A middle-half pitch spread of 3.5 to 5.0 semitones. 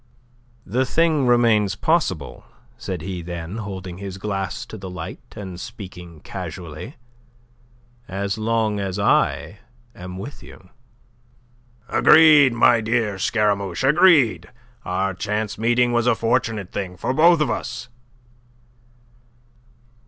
Yes: average, 4.4 semitones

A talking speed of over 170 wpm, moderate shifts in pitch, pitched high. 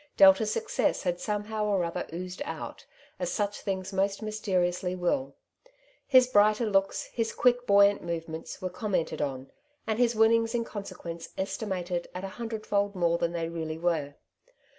No: average, 155 wpm; average, 3.7 semitones; high, 195 Hz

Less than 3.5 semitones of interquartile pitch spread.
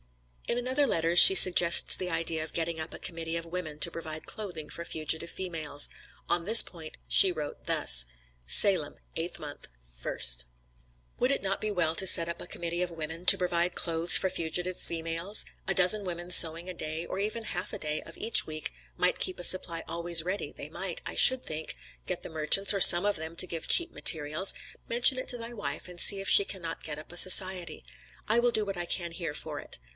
Yes: average, 2.9 semitones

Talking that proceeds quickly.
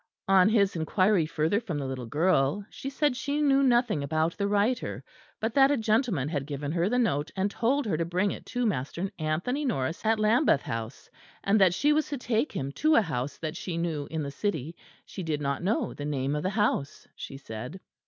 Yes: fast, 215 wpm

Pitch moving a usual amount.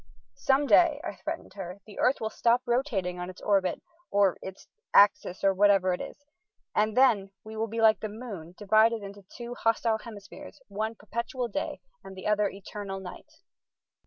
Yes: average, 3.1 semitones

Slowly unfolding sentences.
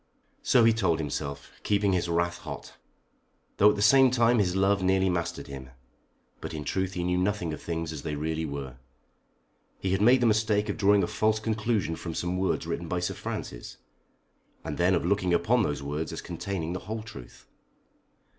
No: average, 195 wpm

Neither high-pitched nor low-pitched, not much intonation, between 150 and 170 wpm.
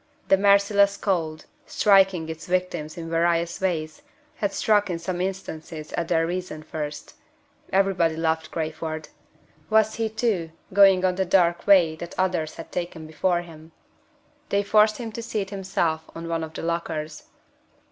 No: medium, 175 Hz; average, 3.3 semitones; average, 155 wpm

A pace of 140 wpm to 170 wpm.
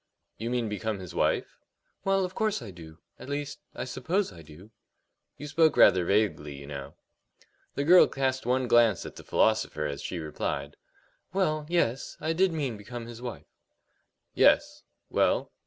Yes: average, 165 wpm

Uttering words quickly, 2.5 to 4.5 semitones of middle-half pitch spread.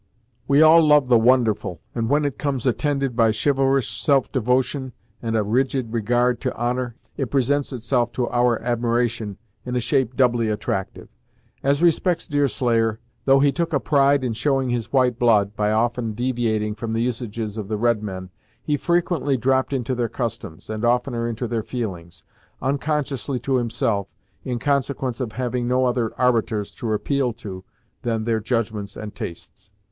No: average, 165 wpm; average, 3.0 semitones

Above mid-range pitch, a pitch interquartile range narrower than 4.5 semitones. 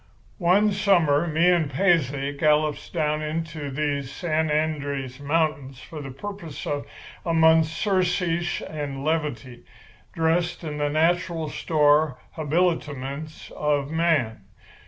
No: medium, 155 Hz; narrow, 2.6 semitones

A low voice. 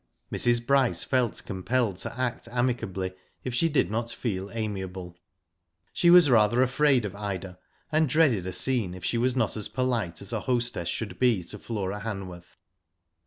Yes: low, 115 Hz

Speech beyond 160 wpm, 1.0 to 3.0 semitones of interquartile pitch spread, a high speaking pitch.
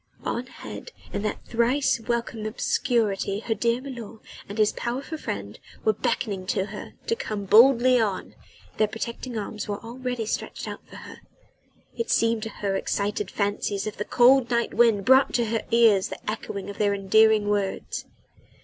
Yes: average, 170 wpm; average, 2.7 semitones; high, 220 Hz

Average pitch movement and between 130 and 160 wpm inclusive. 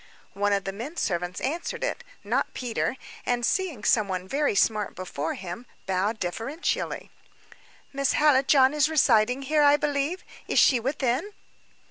No: wide, 6.2 semitones; average, 140 wpm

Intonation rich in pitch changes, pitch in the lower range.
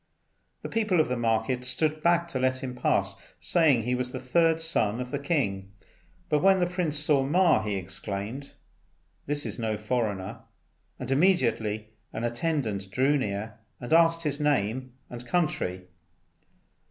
Yes: wide, 6.0 semitones; low, 130 Hz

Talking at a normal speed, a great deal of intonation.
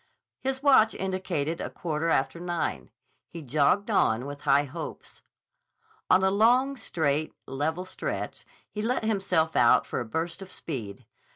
Yes: average, 150 wpm; wide, 5.8 semitones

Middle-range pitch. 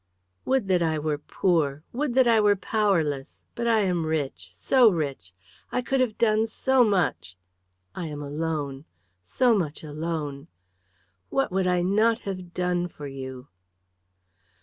Yes: medium, 175 Hz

